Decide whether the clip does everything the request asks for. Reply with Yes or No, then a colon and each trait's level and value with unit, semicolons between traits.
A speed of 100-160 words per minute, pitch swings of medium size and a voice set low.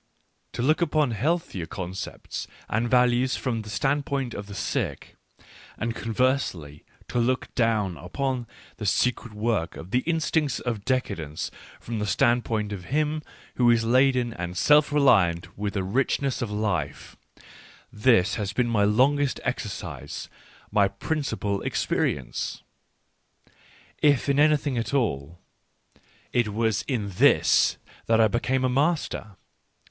Yes: slow, 135 wpm; average, 4.5 semitones; low, 120 Hz